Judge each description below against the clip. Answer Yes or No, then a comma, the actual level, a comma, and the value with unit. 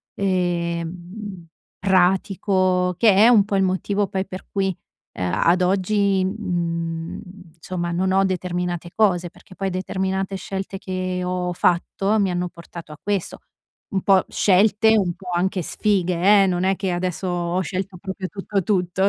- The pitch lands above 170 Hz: Yes, medium, 185 Hz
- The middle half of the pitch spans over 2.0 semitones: No, narrow, 1.7 semitones